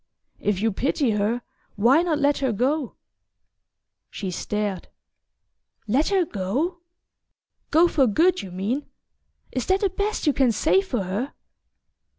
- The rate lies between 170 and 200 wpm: No, average, 140 wpm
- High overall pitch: Yes, very high, 265 Hz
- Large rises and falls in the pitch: Yes, wide, 7.4 semitones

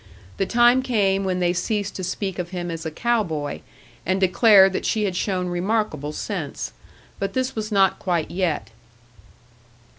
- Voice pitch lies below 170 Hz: No, high, 190 Hz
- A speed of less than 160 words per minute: No, average, 170 wpm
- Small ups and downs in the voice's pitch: No, average, 3.3 semitones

